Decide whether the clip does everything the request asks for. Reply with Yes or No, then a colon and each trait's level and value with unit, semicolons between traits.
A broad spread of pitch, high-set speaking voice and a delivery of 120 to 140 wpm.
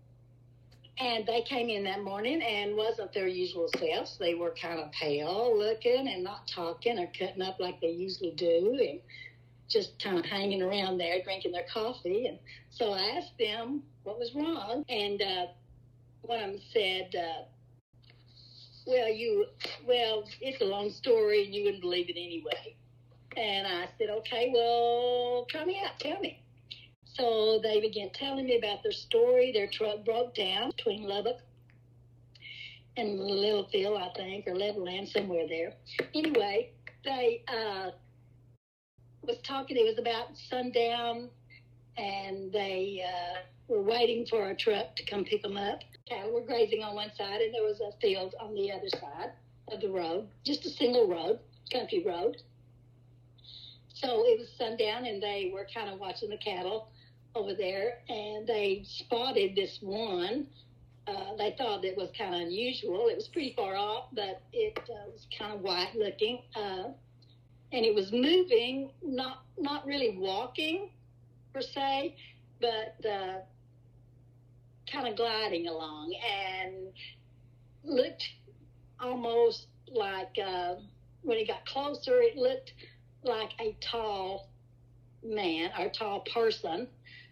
No: wide, 7.6 semitones; high, 205 Hz; average, 150 wpm